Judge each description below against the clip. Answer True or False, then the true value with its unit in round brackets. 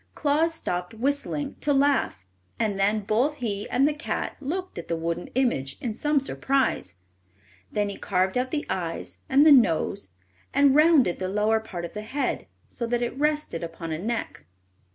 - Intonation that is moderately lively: False (7.3 semitones)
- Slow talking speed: False (175 wpm)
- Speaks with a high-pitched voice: True (235 Hz)